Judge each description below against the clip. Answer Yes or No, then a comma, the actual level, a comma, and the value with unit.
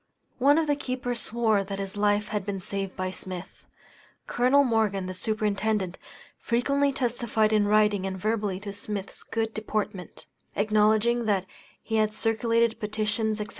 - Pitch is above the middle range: Yes, high, 215 Hz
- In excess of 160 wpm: No, average, 150 wpm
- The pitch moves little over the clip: Yes, narrow, 2.3 semitones